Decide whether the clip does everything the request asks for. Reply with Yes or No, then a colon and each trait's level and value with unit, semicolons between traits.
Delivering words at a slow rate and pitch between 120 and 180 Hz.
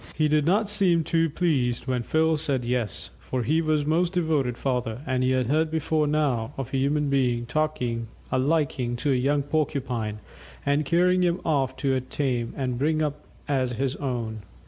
No: average, 185 wpm; medium, 140 Hz